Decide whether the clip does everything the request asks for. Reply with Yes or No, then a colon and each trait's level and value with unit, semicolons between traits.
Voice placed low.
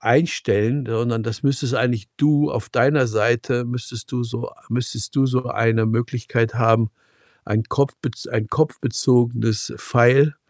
Yes: low, 120 Hz